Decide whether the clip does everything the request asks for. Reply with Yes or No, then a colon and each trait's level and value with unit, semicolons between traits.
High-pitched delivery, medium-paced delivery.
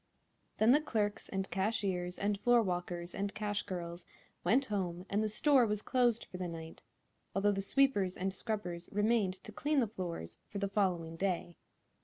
Yes: high, 200 Hz; average, 170 wpm